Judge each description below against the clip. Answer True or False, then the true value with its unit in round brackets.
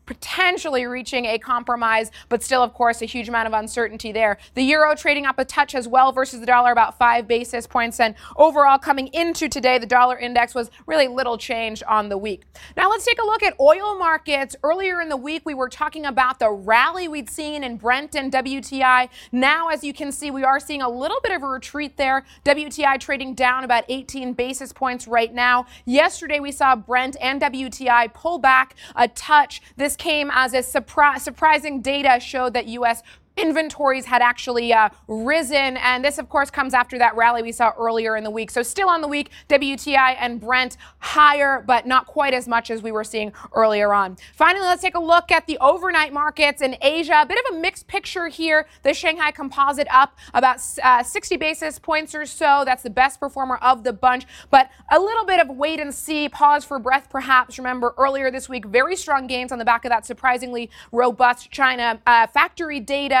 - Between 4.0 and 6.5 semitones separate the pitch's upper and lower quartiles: False (3.4 semitones)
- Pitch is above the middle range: True (265 Hz)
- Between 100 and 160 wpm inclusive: False (205 wpm)